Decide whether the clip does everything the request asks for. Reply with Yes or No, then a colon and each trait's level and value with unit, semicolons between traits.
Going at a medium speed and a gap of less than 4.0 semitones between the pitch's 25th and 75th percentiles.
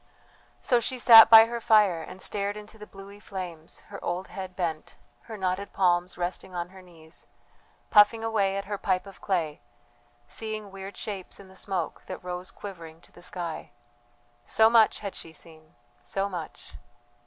Yes: average, 170 wpm; average, 2.9 semitones